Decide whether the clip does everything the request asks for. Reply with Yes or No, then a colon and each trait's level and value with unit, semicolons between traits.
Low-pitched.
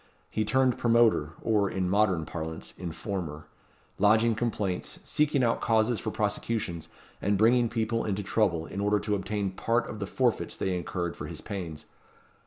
Yes: low, 105 Hz